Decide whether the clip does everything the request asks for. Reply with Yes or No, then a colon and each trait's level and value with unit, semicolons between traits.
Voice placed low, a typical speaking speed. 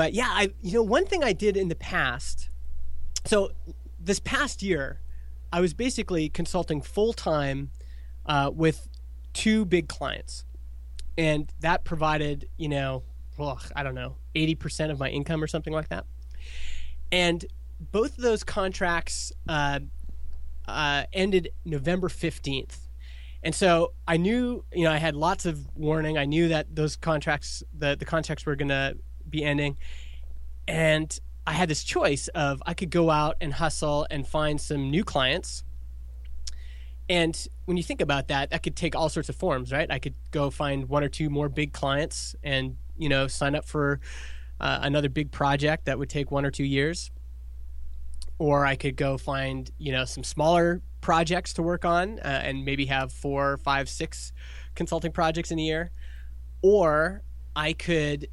No: medium, 145 Hz; average, 170 wpm